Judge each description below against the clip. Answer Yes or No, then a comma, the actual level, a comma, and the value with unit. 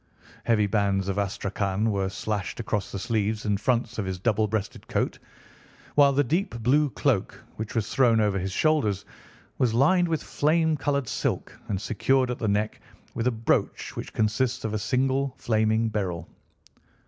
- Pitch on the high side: No, low, 110 Hz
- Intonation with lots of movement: No, average, 4.3 semitones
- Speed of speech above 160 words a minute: Yes, average, 170 wpm